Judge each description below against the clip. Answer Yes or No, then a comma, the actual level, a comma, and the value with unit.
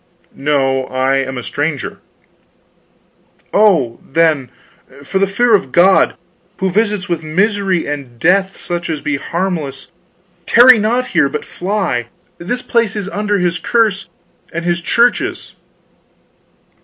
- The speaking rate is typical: No, slow, 130 wpm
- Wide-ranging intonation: Yes, wide, 5.9 semitones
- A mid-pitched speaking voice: Yes, medium, 175 Hz